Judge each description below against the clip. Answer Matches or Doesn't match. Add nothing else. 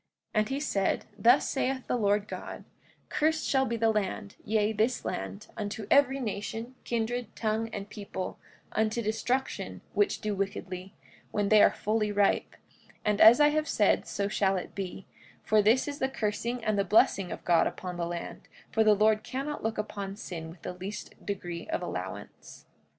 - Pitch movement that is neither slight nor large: Matches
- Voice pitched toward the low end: Doesn't match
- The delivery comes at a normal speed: Matches